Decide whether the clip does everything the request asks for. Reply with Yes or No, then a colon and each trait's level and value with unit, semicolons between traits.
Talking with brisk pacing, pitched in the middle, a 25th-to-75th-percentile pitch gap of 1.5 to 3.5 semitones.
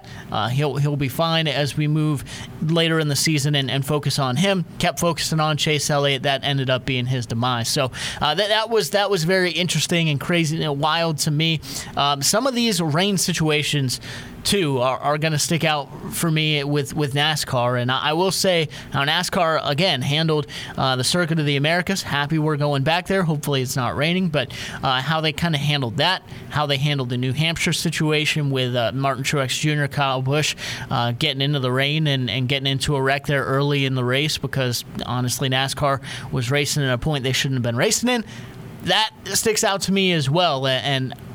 Yes: fast, 210 wpm; medium, 145 Hz; average, 3.1 semitones